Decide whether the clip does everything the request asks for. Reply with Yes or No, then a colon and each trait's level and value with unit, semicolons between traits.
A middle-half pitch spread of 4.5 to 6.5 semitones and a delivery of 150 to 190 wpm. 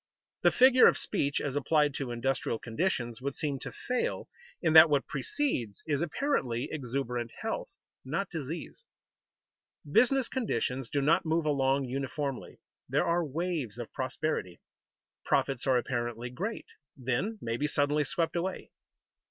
No: average, 4.8 semitones; average, 140 wpm